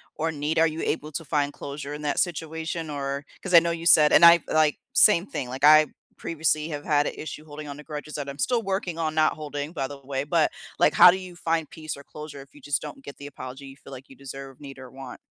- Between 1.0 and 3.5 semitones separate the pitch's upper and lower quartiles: Yes, narrow, 2.5 semitones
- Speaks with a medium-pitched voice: Yes, medium, 150 Hz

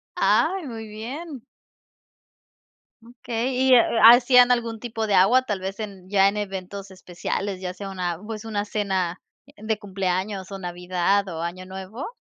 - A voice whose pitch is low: No, high, 205 Hz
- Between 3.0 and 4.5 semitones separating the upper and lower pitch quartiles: Yes, average, 3.4 semitones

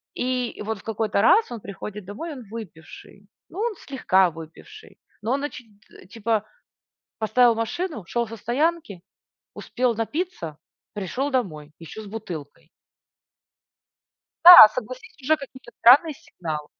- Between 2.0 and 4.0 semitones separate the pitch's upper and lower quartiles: No, average, 5.3 semitones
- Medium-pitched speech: No, high, 225 Hz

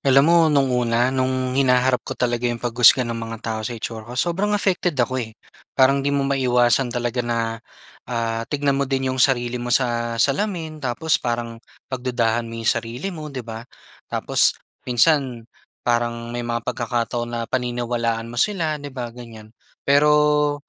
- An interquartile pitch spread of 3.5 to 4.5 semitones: No, average, 2.7 semitones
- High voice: No, low, 125 Hz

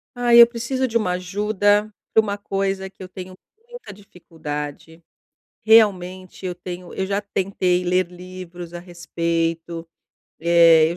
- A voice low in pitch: No, medium, 185 Hz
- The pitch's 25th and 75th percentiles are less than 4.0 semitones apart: Yes, average, 2.9 semitones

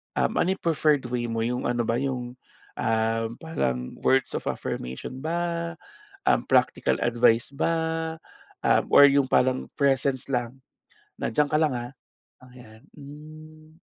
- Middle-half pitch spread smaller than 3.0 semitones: No, average, 4.5 semitones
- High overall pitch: No, low, 135 Hz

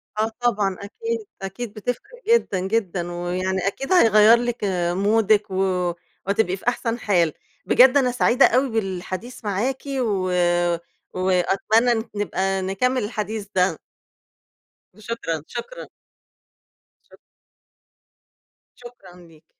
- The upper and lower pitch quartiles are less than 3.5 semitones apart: No, average, 4.3 semitones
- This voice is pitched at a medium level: No, high, 210 Hz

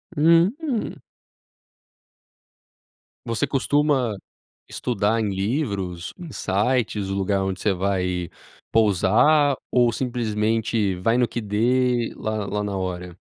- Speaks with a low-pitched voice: Yes, low, 110 Hz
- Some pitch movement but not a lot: Yes, average, 4.5 semitones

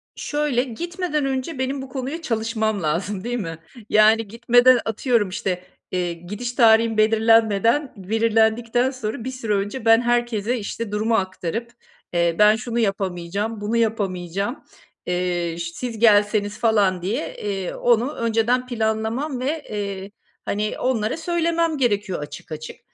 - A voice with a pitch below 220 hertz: No, high, 225 Hz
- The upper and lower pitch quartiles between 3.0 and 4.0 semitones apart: Yes, average, 3.4 semitones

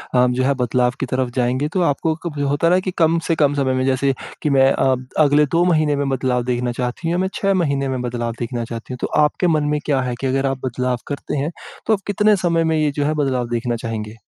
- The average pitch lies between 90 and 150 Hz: Yes, low, 135 Hz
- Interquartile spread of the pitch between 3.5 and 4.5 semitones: Yes, average, 3.8 semitones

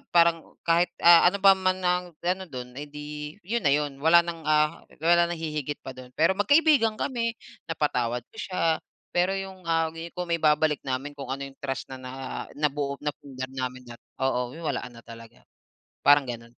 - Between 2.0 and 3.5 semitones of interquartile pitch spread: No, average, 4.5 semitones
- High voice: No, medium, 155 Hz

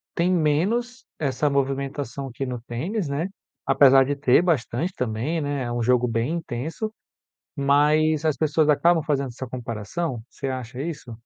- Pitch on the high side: No, medium, 140 Hz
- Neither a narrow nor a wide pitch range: Yes, average, 4.0 semitones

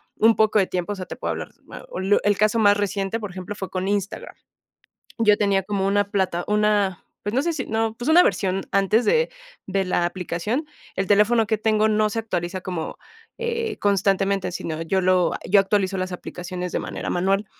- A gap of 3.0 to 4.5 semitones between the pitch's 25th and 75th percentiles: No, narrow, 2.4 semitones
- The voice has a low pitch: No, high, 200 Hz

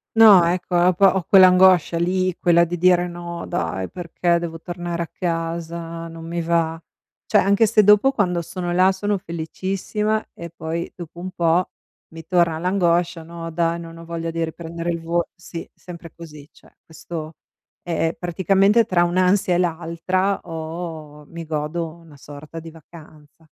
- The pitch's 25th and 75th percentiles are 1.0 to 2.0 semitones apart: Yes, narrow, 1.7 semitones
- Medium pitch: Yes, medium, 170 Hz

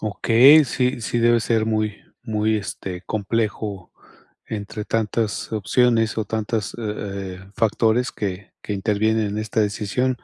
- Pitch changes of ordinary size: No, narrow, 1.9 semitones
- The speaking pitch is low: Yes, low, 110 Hz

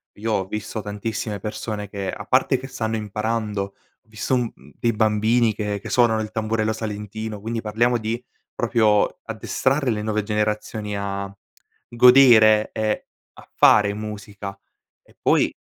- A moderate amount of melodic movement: No, narrow, 1.5 semitones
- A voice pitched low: Yes, low, 110 Hz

